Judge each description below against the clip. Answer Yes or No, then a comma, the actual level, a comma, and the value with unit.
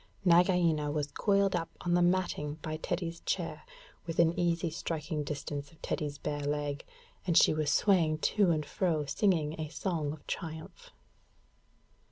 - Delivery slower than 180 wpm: Yes, average, 150 wpm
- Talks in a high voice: No, medium, 160 Hz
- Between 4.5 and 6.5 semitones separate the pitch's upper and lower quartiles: No, average, 2.8 semitones